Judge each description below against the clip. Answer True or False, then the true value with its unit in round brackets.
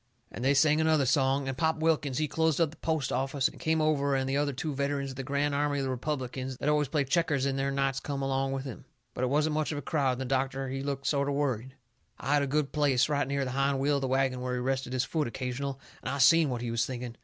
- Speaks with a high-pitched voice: False (140 Hz)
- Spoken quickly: True (280 wpm)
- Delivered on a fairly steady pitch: True (1.8 semitones)